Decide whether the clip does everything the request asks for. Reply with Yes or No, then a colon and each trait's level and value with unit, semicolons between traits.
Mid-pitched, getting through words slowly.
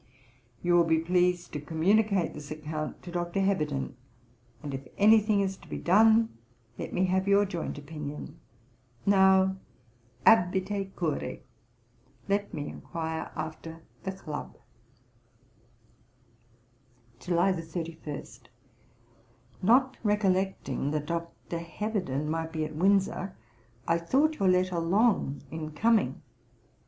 Yes: medium, 175 Hz; slow, 115 wpm